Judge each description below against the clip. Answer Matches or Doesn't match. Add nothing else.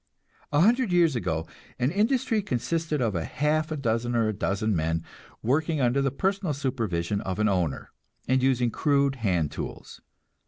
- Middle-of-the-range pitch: Doesn't match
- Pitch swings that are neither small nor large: Doesn't match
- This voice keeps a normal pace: Matches